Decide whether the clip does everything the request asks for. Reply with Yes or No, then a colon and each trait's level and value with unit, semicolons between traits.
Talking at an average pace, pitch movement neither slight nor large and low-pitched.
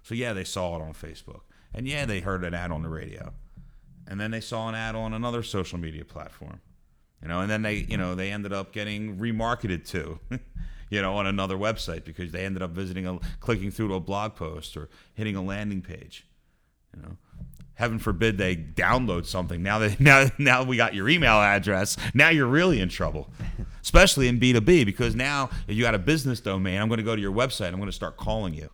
No: fast, 225 wpm; average, 4.2 semitones; low, 100 Hz